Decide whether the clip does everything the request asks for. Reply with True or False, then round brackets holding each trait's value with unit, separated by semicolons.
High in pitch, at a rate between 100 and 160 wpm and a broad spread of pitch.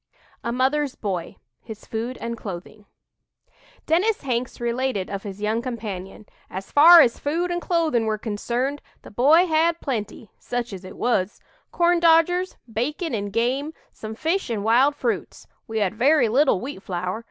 True (240 Hz; 155 wpm; 6.0 semitones)